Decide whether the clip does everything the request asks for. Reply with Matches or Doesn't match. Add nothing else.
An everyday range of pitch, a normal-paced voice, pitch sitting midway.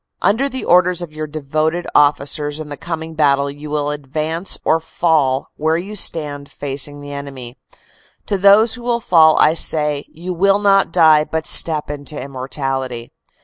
Matches